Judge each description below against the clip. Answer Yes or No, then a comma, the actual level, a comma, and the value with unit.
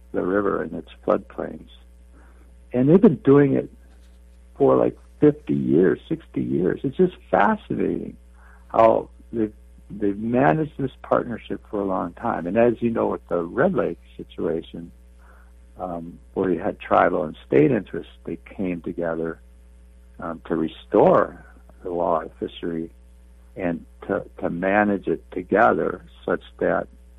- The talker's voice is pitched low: Yes, very low, 80 Hz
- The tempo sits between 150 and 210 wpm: No, average, 140 wpm